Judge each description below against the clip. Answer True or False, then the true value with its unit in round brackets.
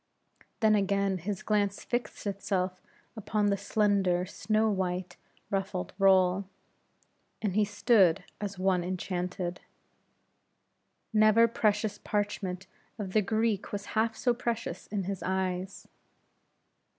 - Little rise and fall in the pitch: True (2.3 semitones)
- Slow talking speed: True (115 wpm)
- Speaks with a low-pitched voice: False (200 Hz)